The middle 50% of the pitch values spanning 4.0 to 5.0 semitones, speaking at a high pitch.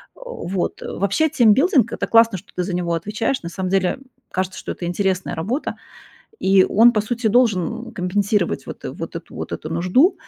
Yes: average, 4.5 semitones; high, 200 Hz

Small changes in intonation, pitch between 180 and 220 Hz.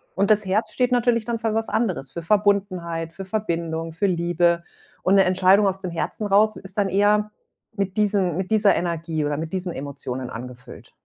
No: average, 3.7 semitones; high, 190 Hz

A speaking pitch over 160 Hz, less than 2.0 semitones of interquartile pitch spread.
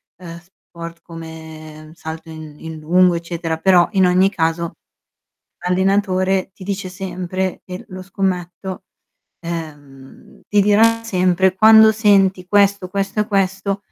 No: medium, 185 Hz; average, 2.7 semitones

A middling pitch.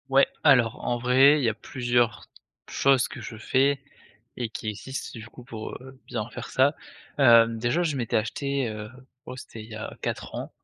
No: low, 120 Hz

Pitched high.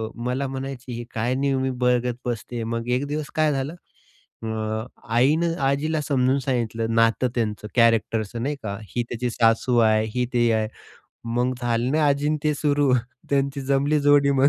No: low, 125 Hz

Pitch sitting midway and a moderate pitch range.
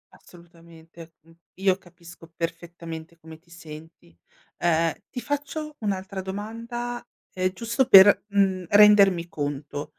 Yes: medium, 175 Hz; average, 3.7 semitones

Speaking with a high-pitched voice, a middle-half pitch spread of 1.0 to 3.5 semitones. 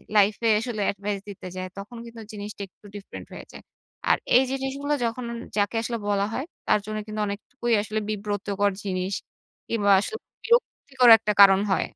Yes: high, 210 Hz; average, 2.8 semitones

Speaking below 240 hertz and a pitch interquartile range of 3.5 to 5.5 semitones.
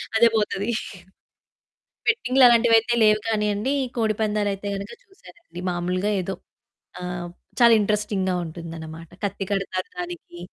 Yes: high, 205 Hz; average, 3.8 semitones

